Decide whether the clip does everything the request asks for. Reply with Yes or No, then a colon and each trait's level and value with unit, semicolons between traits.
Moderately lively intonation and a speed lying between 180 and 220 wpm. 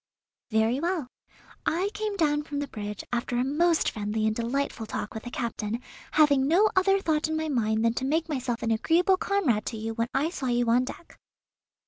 No: wide, 5.9 semitones; average, 200 wpm